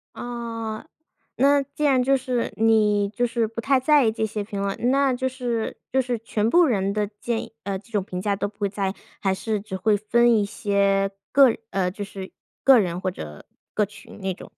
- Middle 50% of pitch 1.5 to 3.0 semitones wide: No, average, 3.5 semitones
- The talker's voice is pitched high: Yes, high, 220 Hz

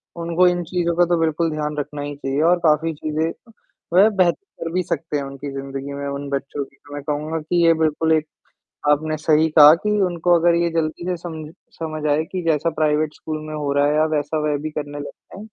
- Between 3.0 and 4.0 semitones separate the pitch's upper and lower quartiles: No, narrow, 2.4 semitones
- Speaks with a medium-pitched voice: Yes, medium, 155 Hz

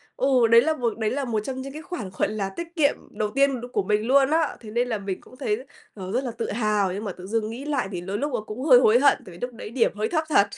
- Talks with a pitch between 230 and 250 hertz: Yes, high, 235 Hz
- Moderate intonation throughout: Yes, average, 4.4 semitones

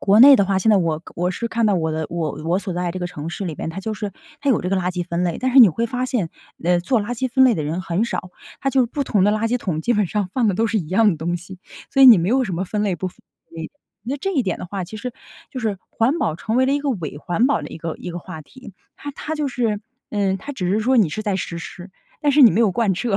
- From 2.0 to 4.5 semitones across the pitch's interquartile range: No, wide, 5.5 semitones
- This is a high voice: Yes, high, 205 Hz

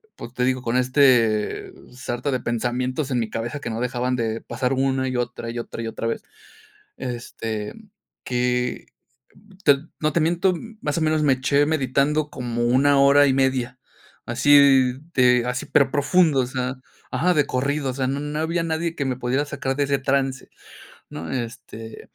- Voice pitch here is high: No, low, 130 Hz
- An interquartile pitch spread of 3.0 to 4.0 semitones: No, narrow, 2.6 semitones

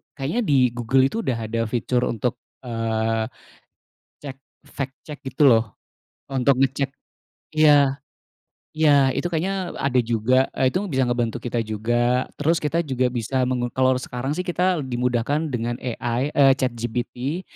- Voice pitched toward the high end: No, low, 130 Hz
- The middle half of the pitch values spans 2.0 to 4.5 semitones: Yes, average, 2.9 semitones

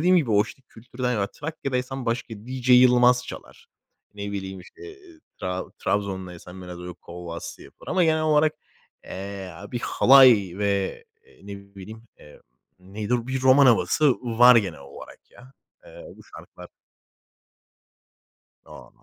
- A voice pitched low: Yes, low, 115 Hz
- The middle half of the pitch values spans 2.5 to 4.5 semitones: No, average, 5.2 semitones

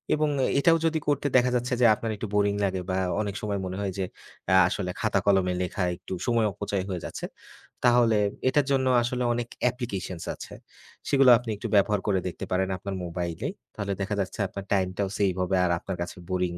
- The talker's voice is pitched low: Yes, low, 100 Hz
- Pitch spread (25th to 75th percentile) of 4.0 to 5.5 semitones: Yes, average, 4.4 semitones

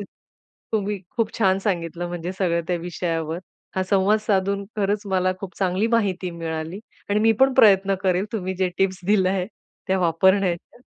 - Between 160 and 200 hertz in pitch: Yes, high, 190 Hz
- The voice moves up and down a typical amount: No, narrow, 2.2 semitones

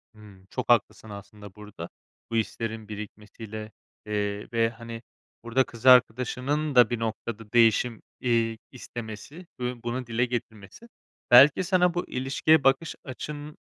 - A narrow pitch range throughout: No, average, 3.0 semitones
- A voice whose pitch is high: No, low, 115 Hz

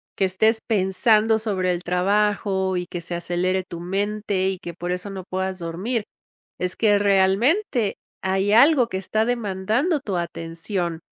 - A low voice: No, high, 190 Hz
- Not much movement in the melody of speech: No, average, 3.0 semitones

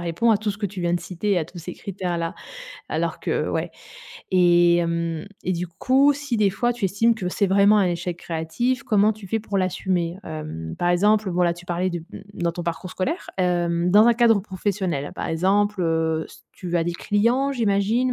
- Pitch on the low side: No, medium, 185 Hz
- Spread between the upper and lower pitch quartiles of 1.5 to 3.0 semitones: No, average, 3.5 semitones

